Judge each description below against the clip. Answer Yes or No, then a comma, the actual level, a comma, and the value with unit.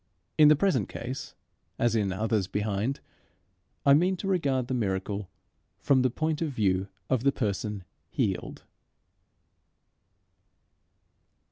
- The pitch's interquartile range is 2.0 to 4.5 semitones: No, wide, 5.5 semitones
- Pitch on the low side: Yes, low, 120 Hz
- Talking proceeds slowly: Yes, slow, 120 wpm